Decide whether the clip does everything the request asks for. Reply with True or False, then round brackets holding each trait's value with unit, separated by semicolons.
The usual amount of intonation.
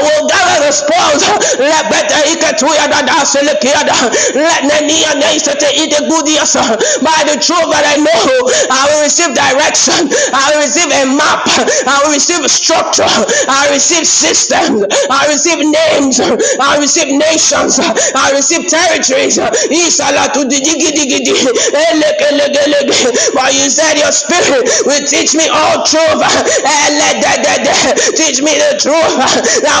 False (1.8 semitones)